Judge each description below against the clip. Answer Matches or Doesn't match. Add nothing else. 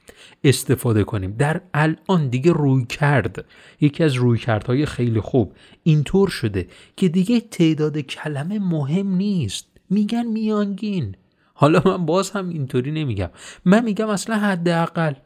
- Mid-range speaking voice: Matches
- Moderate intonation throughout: Doesn't match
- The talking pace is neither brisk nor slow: Matches